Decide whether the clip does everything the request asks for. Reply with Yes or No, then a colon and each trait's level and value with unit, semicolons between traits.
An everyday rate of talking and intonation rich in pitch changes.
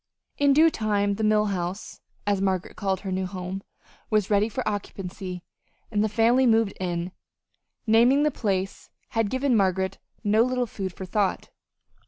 No: average, 160 wpm; average, 3.0 semitones